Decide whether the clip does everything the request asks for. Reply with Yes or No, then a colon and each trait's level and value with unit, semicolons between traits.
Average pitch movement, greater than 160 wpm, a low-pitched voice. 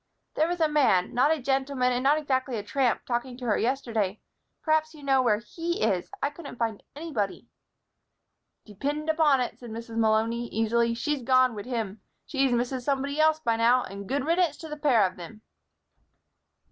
No: average, 4.2 semitones; average, 185 wpm; very high, 255 Hz